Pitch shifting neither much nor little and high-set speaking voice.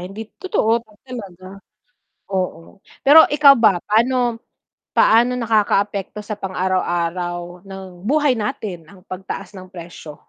Yes: average, 4.1 semitones; high, 195 Hz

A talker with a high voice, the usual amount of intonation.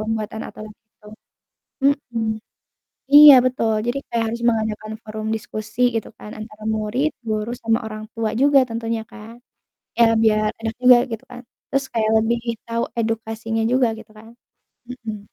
No: high, 225 Hz; narrow, 1.5 semitones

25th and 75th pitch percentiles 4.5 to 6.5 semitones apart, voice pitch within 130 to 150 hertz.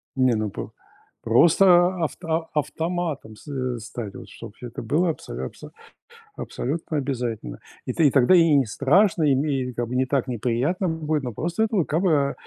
Yes: average, 4.9 semitones; medium, 140 Hz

